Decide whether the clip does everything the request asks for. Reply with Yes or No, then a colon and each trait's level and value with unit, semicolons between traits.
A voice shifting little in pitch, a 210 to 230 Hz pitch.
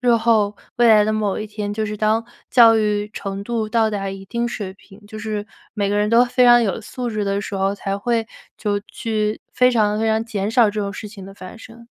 Yes: narrow, 2.0 semitones; high, 215 Hz